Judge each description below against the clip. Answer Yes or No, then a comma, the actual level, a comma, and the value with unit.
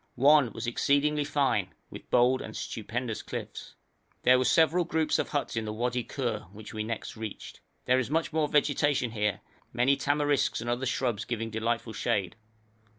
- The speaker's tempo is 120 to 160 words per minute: No, average, 170 wpm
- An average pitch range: Yes, average, 4.3 semitones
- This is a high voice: No, low, 125 Hz